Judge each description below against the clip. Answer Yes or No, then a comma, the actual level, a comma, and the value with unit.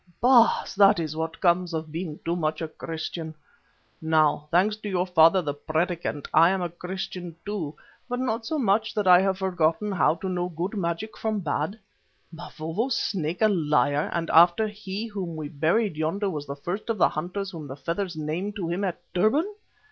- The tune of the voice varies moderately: Yes, average, 4.0 semitones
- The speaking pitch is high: No, medium, 175 Hz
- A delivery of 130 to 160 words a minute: No, average, 195 wpm